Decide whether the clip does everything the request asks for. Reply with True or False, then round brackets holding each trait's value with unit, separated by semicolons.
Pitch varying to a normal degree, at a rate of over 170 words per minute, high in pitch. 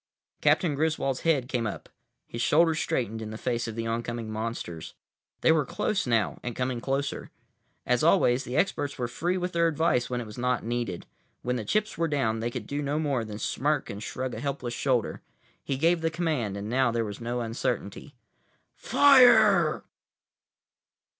False (4.8 semitones; 180 wpm; 125 Hz)